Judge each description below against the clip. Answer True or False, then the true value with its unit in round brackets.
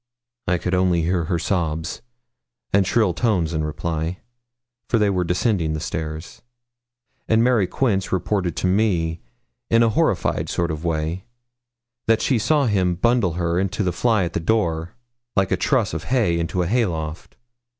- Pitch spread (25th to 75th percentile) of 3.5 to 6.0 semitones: True (4.3 semitones)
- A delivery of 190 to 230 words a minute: False (170 wpm)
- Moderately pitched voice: False (90 Hz)